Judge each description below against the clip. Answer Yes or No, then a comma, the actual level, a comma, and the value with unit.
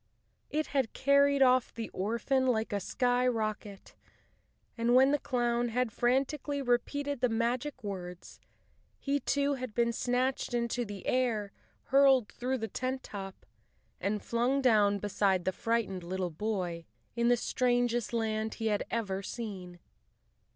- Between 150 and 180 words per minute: No, average, 140 wpm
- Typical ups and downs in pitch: Yes, average, 3.7 semitones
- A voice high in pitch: Yes, high, 235 Hz